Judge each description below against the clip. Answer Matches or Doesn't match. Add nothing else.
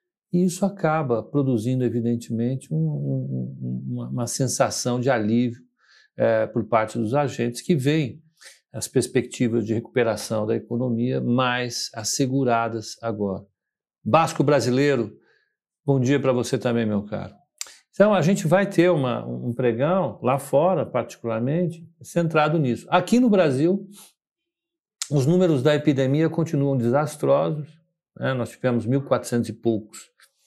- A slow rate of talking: Doesn't match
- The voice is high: Doesn't match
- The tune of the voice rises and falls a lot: Matches